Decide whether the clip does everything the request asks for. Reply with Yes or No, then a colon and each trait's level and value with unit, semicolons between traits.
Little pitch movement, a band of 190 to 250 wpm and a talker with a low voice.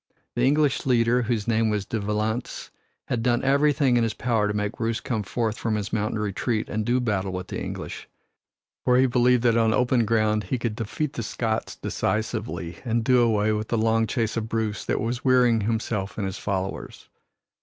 Yes: narrow, 2.3 semitones; average, 195 wpm; low, 115 Hz